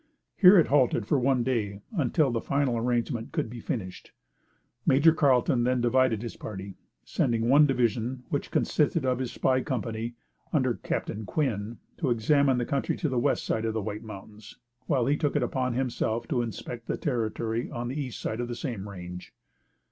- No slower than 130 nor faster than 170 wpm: No, average, 185 wpm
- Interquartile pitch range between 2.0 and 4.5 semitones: Yes, average, 2.9 semitones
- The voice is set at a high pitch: No, low, 120 Hz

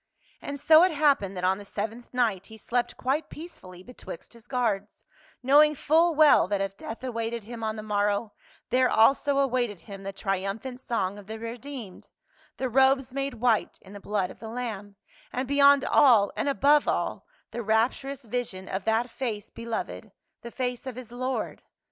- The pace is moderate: Yes, average, 180 wpm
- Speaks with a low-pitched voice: No, high, 235 Hz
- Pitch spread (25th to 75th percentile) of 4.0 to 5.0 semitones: Yes, average, 4.3 semitones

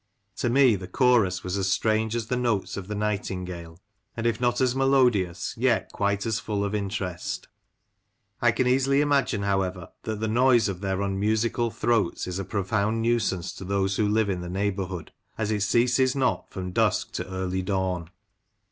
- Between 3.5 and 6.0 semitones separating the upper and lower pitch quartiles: Yes, average, 3.8 semitones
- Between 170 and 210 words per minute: Yes, average, 180 wpm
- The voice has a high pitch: No, low, 105 Hz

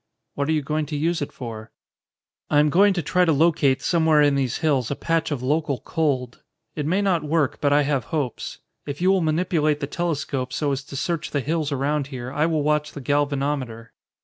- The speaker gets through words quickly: Yes, fast, 215 wpm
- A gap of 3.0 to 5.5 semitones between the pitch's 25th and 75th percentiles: No, narrow, 2.6 semitones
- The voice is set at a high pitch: No, medium, 150 Hz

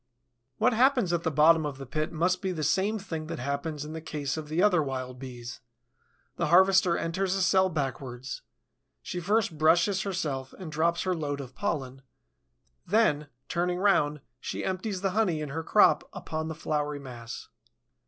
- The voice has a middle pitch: Yes, medium, 160 Hz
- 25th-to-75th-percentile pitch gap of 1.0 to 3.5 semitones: No, average, 4.4 semitones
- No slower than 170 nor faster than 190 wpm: Yes, average, 175 wpm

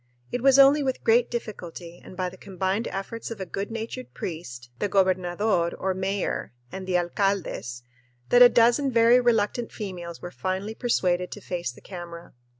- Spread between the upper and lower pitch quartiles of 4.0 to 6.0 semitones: Yes, average, 4.6 semitones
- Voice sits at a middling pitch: No, high, 195 Hz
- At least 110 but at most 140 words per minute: No, average, 170 wpm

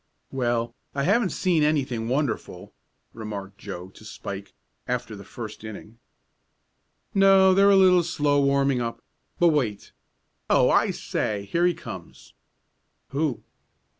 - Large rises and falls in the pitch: Yes, wide, 7.5 semitones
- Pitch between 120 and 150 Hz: Yes, low, 135 Hz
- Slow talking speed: Yes, slow, 130 wpm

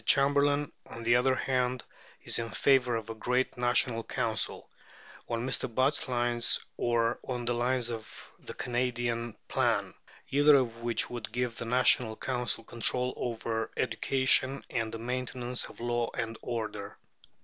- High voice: No, low, 120 Hz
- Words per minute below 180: Yes, average, 150 wpm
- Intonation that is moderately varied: No, narrow, 1.7 semitones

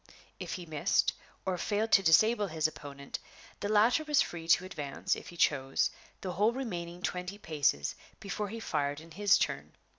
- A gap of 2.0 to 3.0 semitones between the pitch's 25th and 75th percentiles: No, average, 5.0 semitones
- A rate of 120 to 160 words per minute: No, average, 175 wpm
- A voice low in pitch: No, medium, 180 Hz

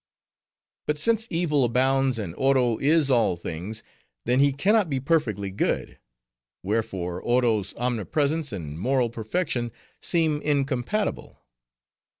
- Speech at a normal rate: No, slow, 120 wpm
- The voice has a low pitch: Yes, low, 130 Hz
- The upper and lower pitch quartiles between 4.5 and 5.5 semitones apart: Yes, average, 5.2 semitones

